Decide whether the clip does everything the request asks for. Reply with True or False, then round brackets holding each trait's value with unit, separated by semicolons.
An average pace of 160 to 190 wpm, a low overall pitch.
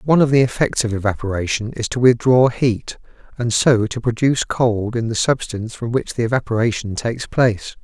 True (185 wpm; 115 Hz)